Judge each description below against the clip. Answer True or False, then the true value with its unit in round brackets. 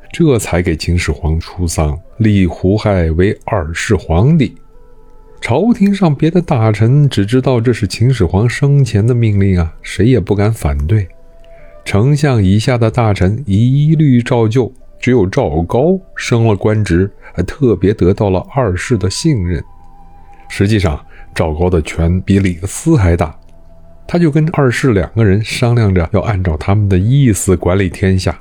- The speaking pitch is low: True (100 Hz)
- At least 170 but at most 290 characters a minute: True (230 characters per minute)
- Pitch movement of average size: False (5.9 semitones)